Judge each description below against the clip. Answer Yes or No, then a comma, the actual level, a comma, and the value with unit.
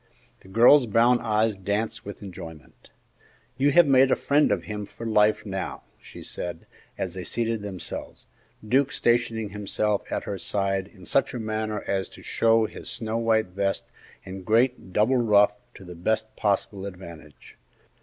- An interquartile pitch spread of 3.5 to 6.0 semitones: No, average, 2.9 semitones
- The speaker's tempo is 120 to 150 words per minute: No, average, 165 wpm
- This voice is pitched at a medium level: No, low, 105 Hz